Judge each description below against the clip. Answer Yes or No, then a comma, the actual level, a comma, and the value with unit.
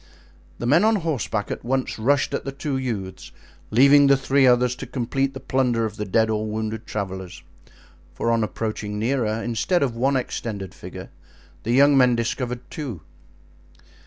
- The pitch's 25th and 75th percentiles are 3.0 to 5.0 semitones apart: Yes, average, 3.8 semitones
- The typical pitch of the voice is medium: No, low, 120 Hz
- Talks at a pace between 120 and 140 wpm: No, average, 165 wpm